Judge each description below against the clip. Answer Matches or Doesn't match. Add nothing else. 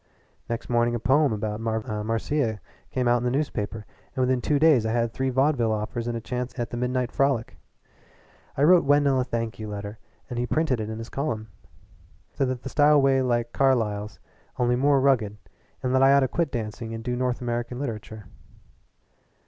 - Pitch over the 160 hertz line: Doesn't match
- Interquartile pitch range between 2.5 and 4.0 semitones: Matches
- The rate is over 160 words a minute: Matches